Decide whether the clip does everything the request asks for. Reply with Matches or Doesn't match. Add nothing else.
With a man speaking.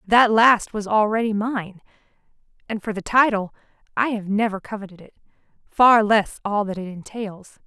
Doesn't match